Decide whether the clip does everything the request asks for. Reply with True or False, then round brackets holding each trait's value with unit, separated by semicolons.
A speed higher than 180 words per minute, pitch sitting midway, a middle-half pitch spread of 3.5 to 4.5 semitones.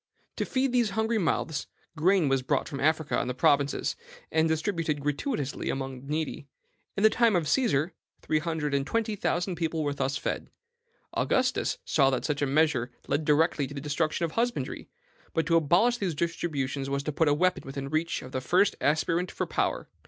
True (195 wpm; 155 Hz; 4.0 semitones)